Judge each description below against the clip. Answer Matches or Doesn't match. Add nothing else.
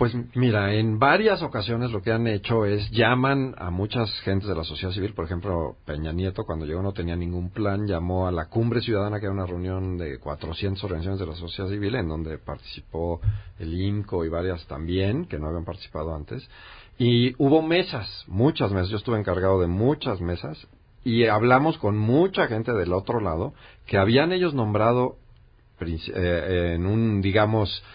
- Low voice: Matches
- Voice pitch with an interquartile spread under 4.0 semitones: Doesn't match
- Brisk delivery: Doesn't match